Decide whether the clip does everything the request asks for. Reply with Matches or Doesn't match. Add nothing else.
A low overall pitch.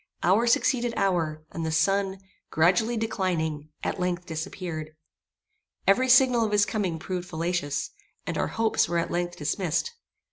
Doesn't match